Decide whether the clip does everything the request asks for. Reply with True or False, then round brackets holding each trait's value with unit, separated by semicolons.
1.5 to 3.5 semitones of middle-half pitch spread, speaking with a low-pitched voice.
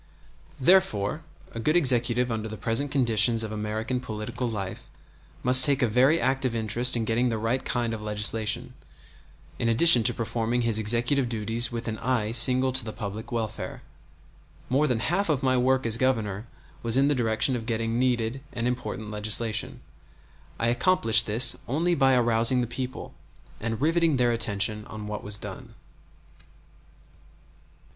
True (2.6 semitones; 115 Hz)